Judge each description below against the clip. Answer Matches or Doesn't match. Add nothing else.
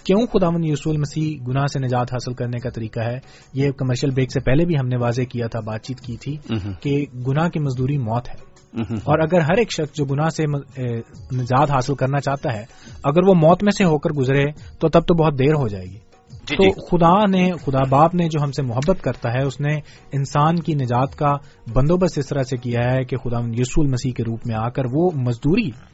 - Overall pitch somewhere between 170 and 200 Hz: Doesn't match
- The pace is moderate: Doesn't match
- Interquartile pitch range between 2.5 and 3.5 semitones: Doesn't match